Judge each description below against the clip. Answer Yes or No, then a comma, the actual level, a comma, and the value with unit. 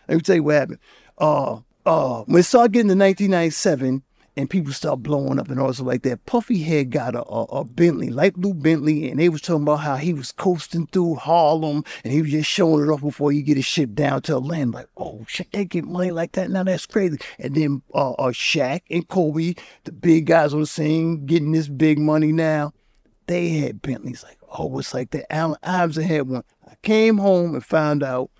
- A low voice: No, medium, 160 Hz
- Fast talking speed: Yes, fast, 220 wpm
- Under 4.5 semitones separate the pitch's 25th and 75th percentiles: Yes, average, 3.0 semitones